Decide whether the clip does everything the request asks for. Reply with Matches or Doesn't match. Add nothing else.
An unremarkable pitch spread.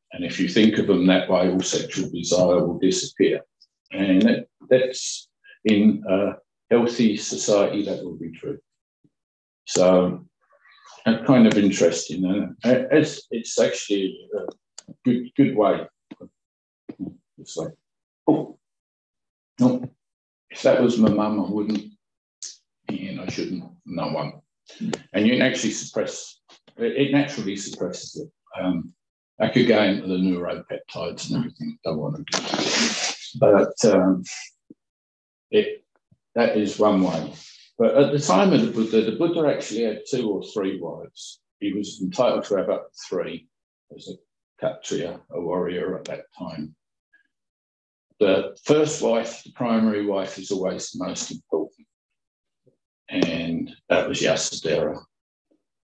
Doesn't match